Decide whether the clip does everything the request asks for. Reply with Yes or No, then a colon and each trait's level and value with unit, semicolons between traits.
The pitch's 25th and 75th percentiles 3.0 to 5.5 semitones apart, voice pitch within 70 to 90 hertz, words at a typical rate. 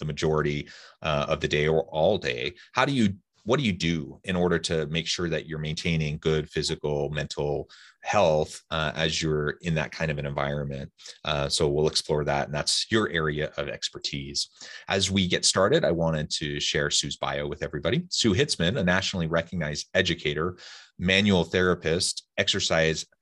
No: narrow, 2.5 semitones; very low, 80 Hz; average, 180 wpm